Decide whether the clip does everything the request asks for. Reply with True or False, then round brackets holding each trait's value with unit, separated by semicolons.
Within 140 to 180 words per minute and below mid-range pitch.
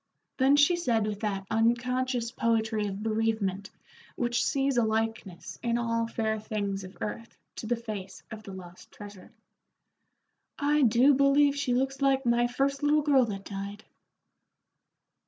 False (150 wpm; 230 Hz)